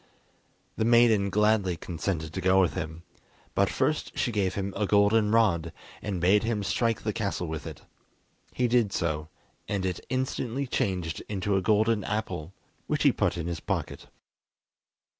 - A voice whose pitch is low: Yes, low, 100 Hz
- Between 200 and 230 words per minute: No, average, 160 wpm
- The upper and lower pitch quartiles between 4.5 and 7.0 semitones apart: No, average, 3.8 semitones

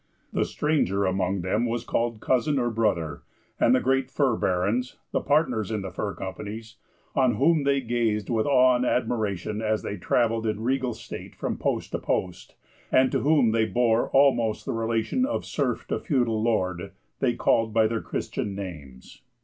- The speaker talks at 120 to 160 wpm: No, average, 175 wpm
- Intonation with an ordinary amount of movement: Yes, average, 3.5 semitones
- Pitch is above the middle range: No, low, 115 Hz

